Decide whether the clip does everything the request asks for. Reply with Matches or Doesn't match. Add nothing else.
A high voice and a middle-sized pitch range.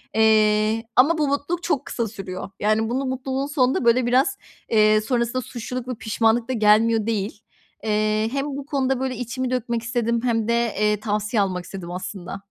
Matches